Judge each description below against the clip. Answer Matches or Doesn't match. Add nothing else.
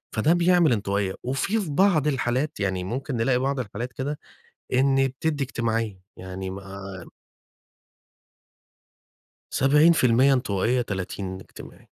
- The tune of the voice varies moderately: Doesn't match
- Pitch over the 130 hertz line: Doesn't match